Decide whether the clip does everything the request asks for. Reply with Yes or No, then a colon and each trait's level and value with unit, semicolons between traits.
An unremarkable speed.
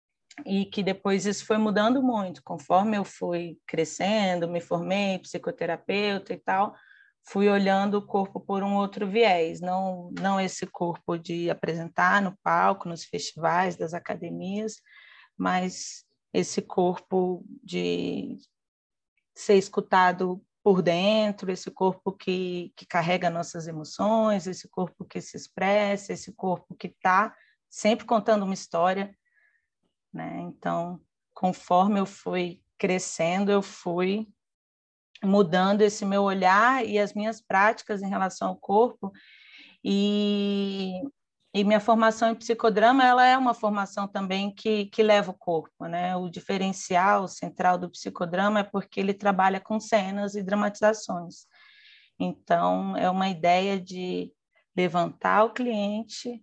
Yes: average, 130 wpm